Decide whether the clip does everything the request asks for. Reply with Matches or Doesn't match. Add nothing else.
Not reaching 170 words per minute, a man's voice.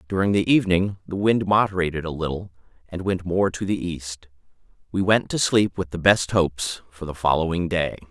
Doesn't match